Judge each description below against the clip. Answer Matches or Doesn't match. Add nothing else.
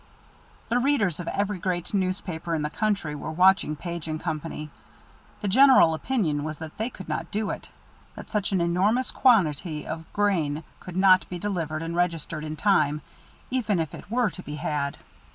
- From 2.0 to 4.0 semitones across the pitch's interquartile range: Doesn't match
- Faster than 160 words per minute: Matches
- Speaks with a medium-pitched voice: Matches